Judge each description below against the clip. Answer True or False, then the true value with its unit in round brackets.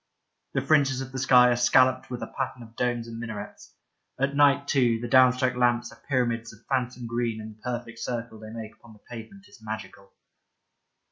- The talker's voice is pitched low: True (120 Hz)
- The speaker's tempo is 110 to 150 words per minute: False (200 wpm)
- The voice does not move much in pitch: True (2.1 semitones)